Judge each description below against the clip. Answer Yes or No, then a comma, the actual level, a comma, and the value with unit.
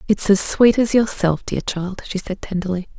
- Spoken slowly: No, average, 200 wpm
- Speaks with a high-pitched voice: Yes, high, 195 Hz